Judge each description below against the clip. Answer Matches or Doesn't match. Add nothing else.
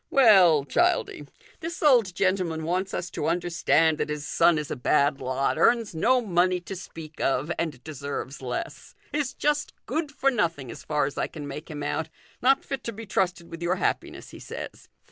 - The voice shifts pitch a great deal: Matches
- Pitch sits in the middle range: Matches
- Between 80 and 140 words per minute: Doesn't match